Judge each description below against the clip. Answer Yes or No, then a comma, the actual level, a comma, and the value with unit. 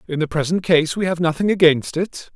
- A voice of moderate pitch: Yes, medium, 170 Hz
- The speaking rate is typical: No, fast, 230 wpm